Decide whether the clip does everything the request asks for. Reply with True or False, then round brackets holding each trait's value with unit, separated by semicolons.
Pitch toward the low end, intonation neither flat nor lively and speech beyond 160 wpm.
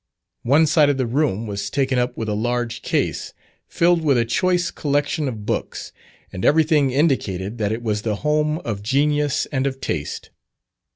True (130 Hz; 5.0 semitones; 175 wpm)